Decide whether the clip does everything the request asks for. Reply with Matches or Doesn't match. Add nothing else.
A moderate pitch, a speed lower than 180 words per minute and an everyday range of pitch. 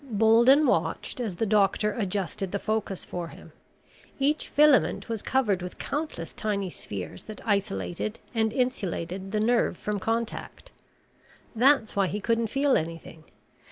Doesn't match